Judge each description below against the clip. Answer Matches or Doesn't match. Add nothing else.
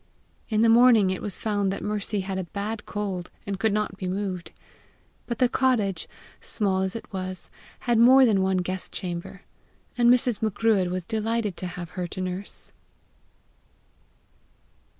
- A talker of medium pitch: Doesn't match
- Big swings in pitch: Doesn't match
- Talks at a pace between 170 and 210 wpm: Doesn't match